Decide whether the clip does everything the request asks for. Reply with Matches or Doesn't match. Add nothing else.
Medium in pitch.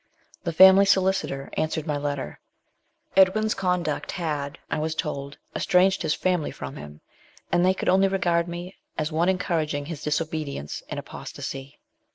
Matches